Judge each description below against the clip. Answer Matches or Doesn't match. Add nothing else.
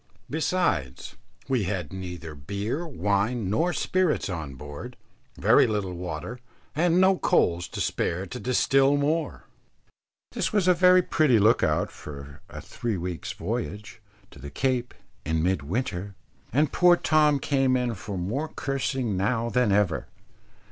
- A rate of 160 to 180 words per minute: Doesn't match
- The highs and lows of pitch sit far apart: Matches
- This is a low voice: Matches